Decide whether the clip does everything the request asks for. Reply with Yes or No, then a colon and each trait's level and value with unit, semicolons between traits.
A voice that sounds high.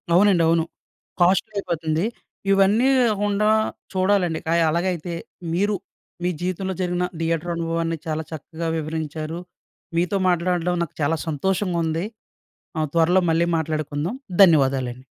No: medium, 170 Hz